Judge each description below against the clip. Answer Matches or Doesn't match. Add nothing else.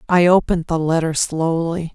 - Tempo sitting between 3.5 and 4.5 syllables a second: Doesn't match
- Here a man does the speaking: Doesn't match